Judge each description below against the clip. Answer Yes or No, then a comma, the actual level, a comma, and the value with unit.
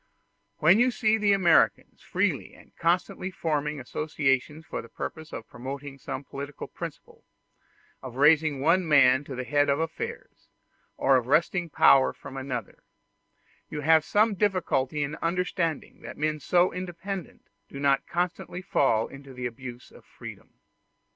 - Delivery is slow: No, average, 145 wpm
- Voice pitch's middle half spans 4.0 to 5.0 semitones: Yes, average, 4.4 semitones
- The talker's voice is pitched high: No, medium, 150 Hz